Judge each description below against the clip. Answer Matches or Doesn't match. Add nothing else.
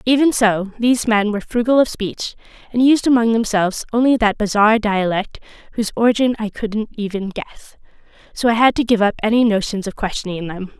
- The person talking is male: Doesn't match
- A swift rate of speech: Doesn't match